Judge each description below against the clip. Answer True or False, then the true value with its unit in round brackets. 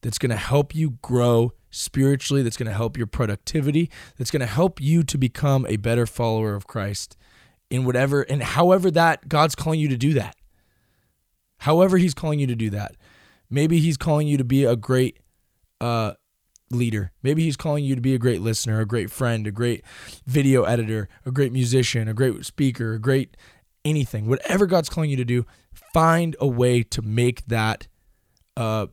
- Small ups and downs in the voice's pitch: False (4.4 semitones)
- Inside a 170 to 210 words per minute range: True (190 wpm)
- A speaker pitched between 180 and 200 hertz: False (125 Hz)